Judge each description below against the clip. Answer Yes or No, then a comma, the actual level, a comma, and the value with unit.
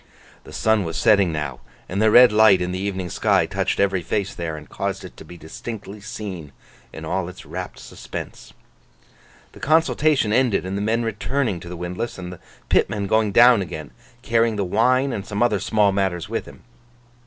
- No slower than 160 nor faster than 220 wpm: Yes, average, 190 wpm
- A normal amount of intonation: Yes, average, 3.8 semitones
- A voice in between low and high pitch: No, low, 100 Hz